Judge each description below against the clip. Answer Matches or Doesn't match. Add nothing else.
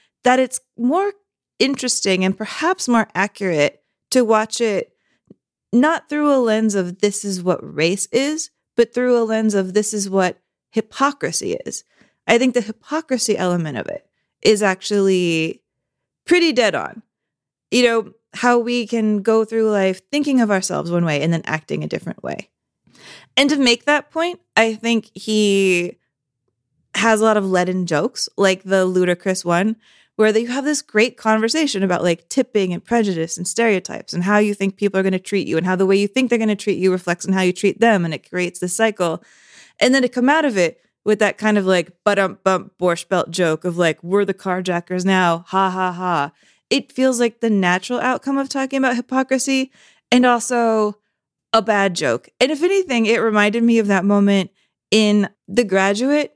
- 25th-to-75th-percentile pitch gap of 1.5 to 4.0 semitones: Doesn't match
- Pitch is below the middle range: Doesn't match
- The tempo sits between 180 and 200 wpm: Matches